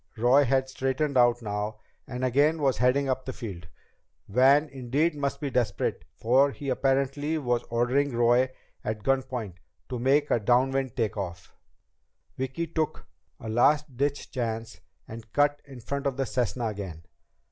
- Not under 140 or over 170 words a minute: Yes, average, 160 wpm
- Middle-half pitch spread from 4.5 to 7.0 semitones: No, average, 3.0 semitones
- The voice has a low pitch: Yes, low, 130 Hz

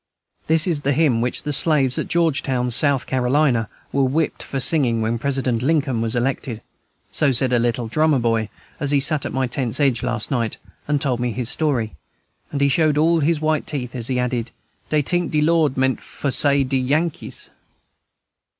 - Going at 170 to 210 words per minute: Yes, average, 190 wpm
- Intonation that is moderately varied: Yes, average, 3.5 semitones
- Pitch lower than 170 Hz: Yes, low, 135 Hz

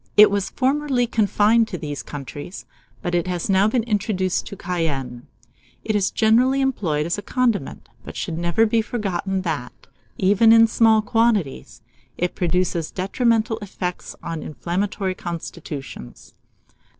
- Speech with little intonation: No, average, 4.6 semitones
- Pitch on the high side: Yes, high, 195 Hz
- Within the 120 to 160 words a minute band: Yes, average, 140 wpm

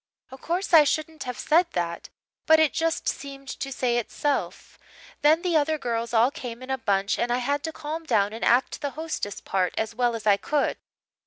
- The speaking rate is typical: No, fast, 210 wpm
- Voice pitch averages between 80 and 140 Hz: No, very high, 265 Hz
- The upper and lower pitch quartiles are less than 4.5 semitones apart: No, average, 5.2 semitones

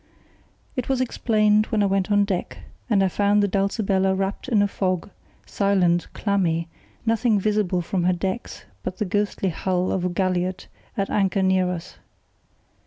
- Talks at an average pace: Yes, average, 165 wpm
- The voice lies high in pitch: Yes, high, 195 Hz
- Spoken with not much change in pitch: Yes, narrow, 2.1 semitones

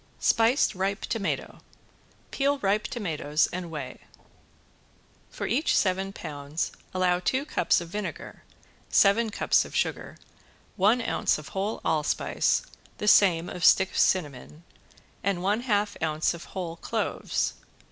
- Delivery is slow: Yes, slow, 125 wpm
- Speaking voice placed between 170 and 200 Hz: Yes, high, 190 Hz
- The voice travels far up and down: No, average, 4.1 semitones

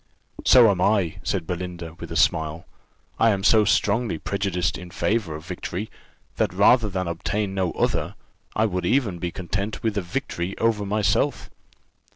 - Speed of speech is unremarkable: Yes, average, 165 wpm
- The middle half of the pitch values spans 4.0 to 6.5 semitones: No, average, 3.4 semitones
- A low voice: Yes, very low, 95 Hz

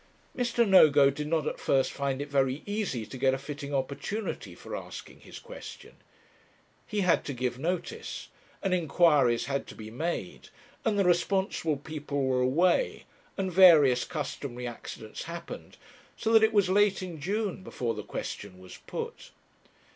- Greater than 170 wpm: No, average, 160 wpm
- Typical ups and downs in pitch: No, wide, 6.0 semitones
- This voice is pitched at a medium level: Yes, medium, 150 Hz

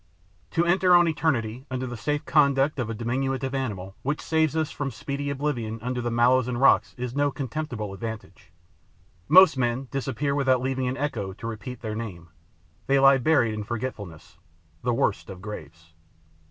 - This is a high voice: No, low, 125 Hz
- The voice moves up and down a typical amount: Yes, average, 4.0 semitones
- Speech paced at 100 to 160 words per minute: No, average, 170 wpm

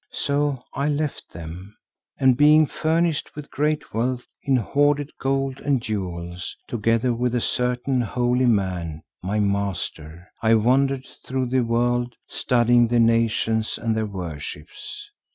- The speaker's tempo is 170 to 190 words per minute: No, slow, 135 wpm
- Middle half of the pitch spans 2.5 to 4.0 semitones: No, average, 4.5 semitones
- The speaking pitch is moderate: No, low, 120 Hz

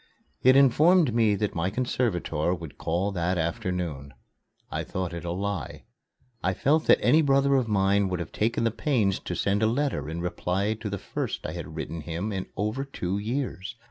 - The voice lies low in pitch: Yes, low, 100 Hz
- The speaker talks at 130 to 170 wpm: No, average, 190 wpm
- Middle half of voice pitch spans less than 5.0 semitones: No, average, 5.3 semitones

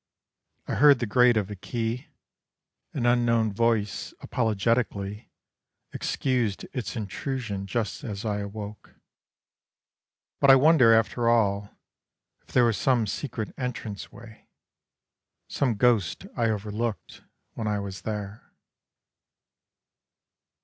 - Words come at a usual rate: No, slow, 110 wpm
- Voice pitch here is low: Yes, low, 115 Hz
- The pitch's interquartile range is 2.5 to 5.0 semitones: Yes, average, 2.9 semitones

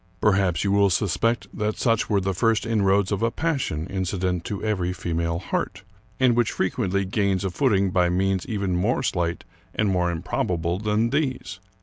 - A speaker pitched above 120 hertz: No, low, 100 Hz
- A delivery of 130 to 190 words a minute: Yes, average, 180 wpm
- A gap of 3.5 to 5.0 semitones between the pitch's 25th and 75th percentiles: No, average, 3.1 semitones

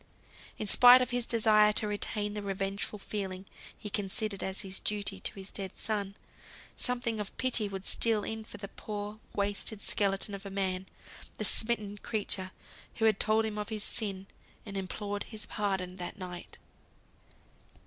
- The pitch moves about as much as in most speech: No, narrow, 1.8 semitones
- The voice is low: No, high, 205 Hz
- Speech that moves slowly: No, average, 165 wpm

